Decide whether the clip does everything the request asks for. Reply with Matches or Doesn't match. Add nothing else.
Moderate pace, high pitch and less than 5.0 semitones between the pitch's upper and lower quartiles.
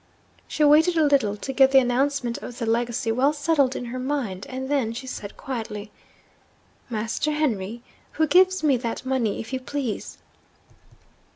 Matches